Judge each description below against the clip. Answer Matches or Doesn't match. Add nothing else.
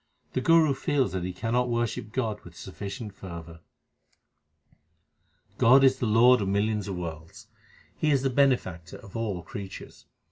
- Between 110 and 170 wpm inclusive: Matches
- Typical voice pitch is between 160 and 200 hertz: Doesn't match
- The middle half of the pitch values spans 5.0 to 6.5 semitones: Matches